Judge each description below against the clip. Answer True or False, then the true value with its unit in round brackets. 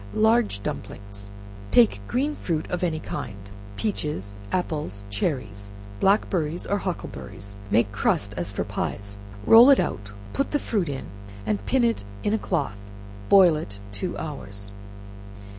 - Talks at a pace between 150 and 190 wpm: False (140 wpm)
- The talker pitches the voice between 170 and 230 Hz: False (135 Hz)